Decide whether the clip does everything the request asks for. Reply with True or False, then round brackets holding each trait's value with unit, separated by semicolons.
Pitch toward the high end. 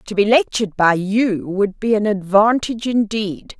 True (210 Hz)